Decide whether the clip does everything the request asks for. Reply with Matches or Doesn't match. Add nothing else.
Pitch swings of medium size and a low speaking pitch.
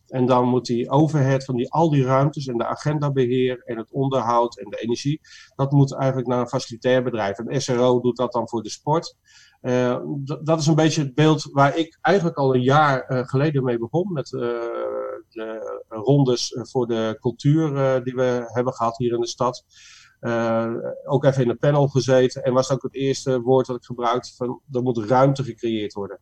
Doesn't match